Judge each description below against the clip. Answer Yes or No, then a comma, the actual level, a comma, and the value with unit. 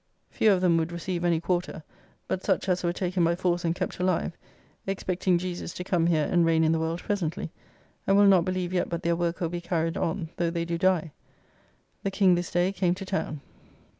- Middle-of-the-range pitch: Yes, medium, 175 Hz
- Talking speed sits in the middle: No, fast, 220 wpm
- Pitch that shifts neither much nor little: No, narrow, 1.6 semitones